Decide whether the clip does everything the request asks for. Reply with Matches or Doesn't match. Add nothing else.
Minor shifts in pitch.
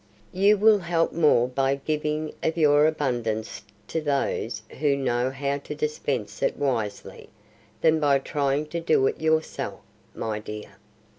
Doesn't match